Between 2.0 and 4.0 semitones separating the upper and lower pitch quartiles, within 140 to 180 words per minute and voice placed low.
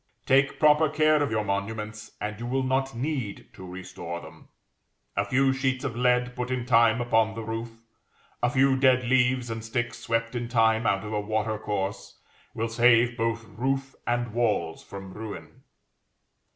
Yes: average, 3.0 semitones; average, 170 wpm; low, 115 Hz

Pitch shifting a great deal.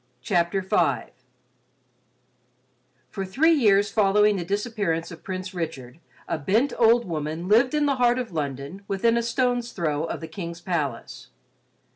Yes: wide, 5.8 semitones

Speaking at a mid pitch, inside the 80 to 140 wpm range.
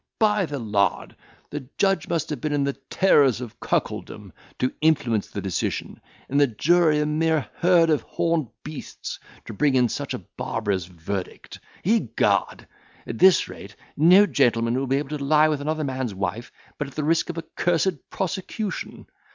No: medium, 145 Hz; average, 175 wpm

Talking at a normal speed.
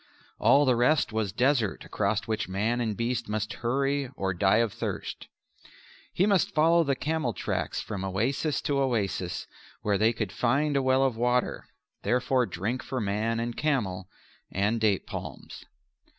Yes: average, 160 wpm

